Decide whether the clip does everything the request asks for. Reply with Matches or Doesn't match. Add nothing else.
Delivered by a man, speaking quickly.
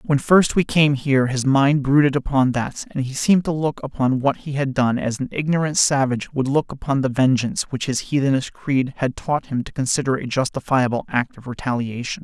Matches